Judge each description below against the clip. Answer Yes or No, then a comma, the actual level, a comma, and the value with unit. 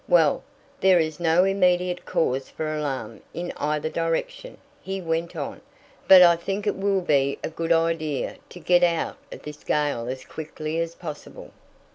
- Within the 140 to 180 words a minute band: Yes, average, 165 wpm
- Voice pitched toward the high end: No, medium, 165 Hz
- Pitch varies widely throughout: No, average, 3.0 semitones